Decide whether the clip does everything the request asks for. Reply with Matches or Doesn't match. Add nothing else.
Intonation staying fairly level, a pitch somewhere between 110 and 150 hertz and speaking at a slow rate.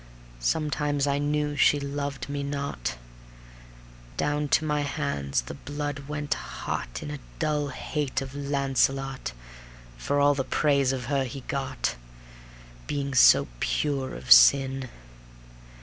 Matches